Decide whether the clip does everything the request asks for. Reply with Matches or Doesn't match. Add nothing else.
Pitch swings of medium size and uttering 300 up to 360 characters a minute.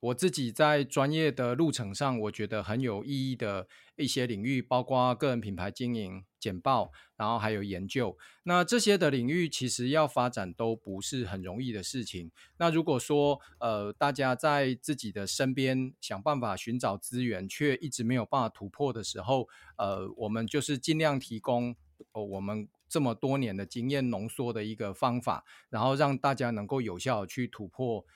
Doesn't match